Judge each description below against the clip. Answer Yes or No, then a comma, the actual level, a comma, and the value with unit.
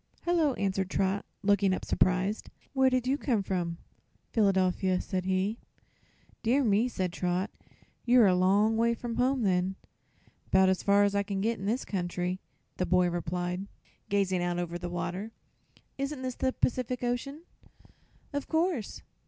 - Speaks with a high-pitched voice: Yes, high, 200 Hz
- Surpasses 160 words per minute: No, average, 155 wpm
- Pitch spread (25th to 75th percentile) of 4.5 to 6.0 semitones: Yes, average, 4.8 semitones